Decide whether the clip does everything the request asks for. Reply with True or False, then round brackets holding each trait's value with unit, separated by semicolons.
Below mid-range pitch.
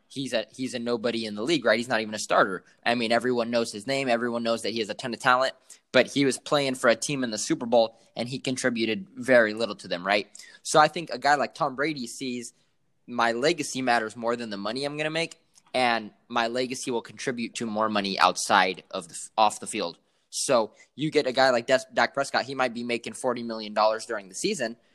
True (120 Hz)